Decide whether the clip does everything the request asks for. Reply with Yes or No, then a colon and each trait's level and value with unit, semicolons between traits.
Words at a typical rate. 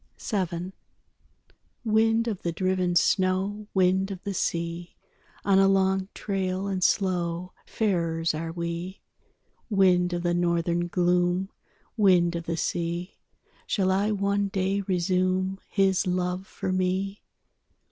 No: slow, 125 wpm